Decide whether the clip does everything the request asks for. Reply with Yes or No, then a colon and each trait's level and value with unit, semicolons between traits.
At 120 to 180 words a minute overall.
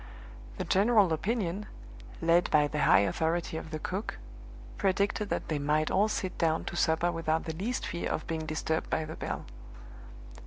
Yes: average, 170 wpm